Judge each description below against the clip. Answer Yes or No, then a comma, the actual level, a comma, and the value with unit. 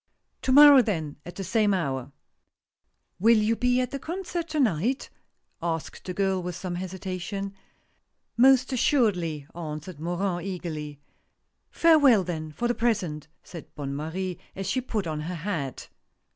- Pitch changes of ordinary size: No, wide, 6.6 semitones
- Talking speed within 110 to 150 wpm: No, average, 160 wpm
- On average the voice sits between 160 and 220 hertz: Yes, medium, 185 Hz